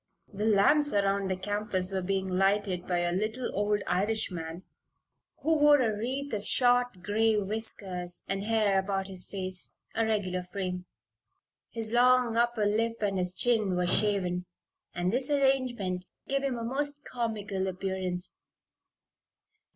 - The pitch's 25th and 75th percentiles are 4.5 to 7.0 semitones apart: No, average, 3.7 semitones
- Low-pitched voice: No, high, 205 Hz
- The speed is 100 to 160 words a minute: Yes, average, 145 wpm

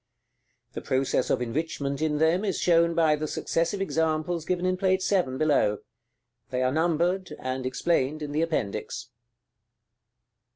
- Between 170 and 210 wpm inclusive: No, average, 140 wpm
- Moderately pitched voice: Yes, medium, 155 Hz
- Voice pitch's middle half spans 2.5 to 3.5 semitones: No, average, 4.1 semitones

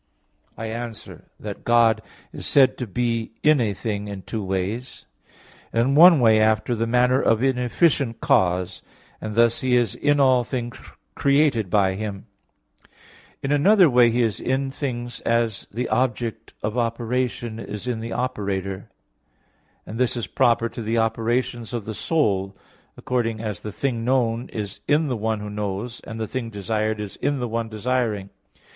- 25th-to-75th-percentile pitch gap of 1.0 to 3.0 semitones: Yes, average, 2.7 semitones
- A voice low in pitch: Yes, low, 115 Hz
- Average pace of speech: Yes, average, 165 wpm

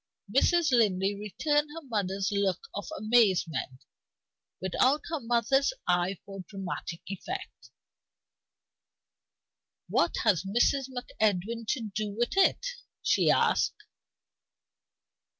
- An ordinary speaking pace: No, slow, 100 wpm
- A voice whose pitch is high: Yes, high, 215 Hz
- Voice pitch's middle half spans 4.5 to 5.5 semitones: Yes, average, 5.0 semitones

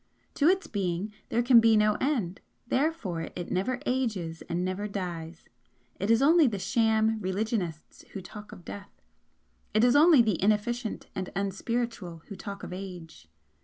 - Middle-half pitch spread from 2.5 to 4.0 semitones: No, average, 4.4 semitones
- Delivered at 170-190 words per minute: No, average, 160 wpm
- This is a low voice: No, high, 210 Hz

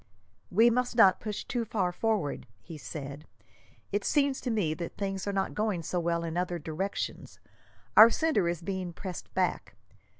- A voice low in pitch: No, high, 190 Hz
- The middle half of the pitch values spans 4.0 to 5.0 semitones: Yes, average, 4.5 semitones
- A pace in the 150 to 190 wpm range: Yes, average, 170 wpm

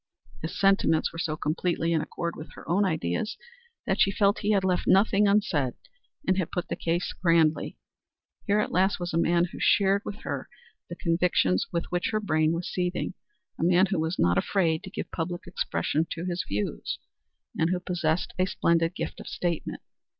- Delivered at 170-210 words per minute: Yes, average, 190 wpm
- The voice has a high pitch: No, medium, 175 Hz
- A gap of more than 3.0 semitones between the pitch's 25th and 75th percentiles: No, average, 2.7 semitones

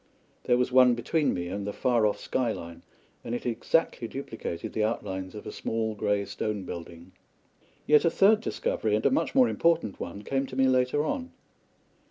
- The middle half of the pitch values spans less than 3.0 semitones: No, average, 5.3 semitones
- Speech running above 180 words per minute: Yes, average, 190 wpm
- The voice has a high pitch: No, low, 120 Hz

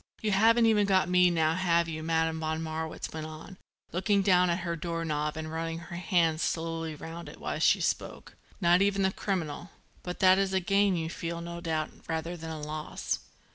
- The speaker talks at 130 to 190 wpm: No, fast, 205 wpm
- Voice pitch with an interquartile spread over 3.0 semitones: No, narrow, 2.5 semitones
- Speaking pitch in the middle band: Yes, medium, 170 Hz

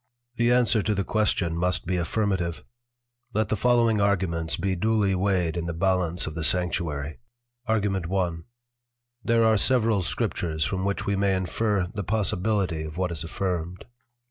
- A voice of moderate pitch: No, very low, 95 Hz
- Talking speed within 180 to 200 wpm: No, average, 165 wpm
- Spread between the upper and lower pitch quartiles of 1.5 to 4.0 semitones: Yes, average, 3.7 semitones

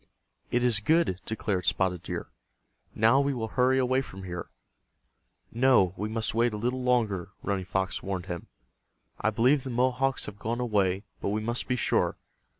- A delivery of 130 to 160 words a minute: No, average, 170 wpm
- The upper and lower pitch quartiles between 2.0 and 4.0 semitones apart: No, average, 4.6 semitones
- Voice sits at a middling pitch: No, low, 110 Hz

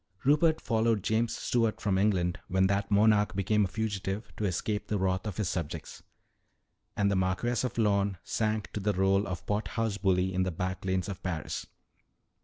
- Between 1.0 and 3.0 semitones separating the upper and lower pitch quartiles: Yes, narrow, 2.5 semitones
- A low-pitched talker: Yes, low, 100 Hz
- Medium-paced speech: Yes, average, 185 wpm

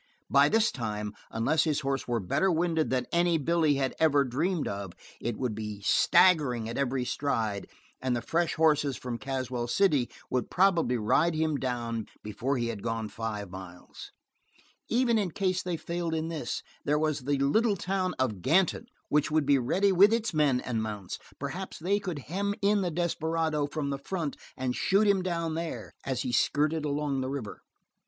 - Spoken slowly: No, average, 185 wpm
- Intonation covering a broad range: Yes, wide, 5.7 semitones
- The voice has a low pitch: No, medium, 145 Hz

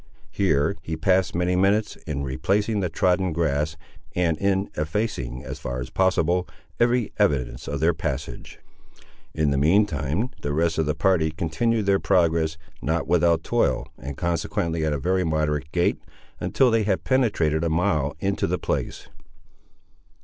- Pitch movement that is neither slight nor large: Yes, average, 4.2 semitones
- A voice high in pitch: No, very low, 85 Hz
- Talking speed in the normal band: Yes, average, 155 wpm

